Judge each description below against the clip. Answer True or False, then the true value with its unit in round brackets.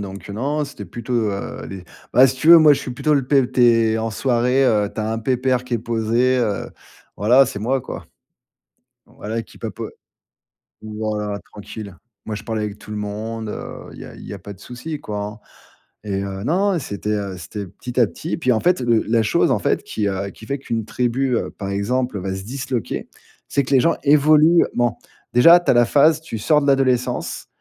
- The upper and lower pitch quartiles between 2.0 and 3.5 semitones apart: False (4.2 semitones)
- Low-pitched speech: True (120 Hz)